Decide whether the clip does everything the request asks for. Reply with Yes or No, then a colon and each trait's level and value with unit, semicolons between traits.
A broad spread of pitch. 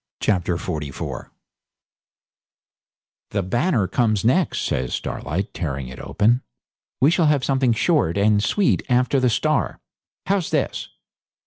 Yes: wide, 7.3 semitones